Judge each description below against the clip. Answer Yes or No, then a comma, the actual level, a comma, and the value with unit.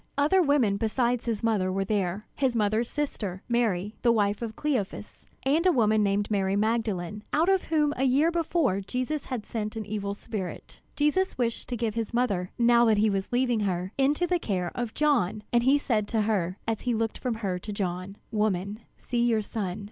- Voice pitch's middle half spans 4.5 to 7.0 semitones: No, average, 3.8 semitones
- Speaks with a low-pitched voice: No, high, 225 Hz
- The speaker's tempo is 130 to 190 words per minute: No, average, 200 wpm